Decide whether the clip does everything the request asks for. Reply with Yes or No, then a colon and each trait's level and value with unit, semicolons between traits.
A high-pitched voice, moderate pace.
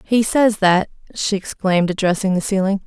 Yes: high, 195 Hz; average, 165 wpm